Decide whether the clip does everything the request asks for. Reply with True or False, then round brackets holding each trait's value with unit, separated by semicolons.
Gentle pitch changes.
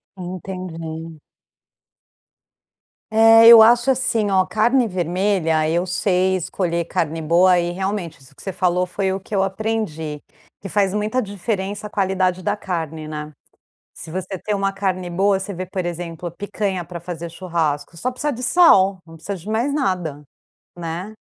False (3.2 semitones)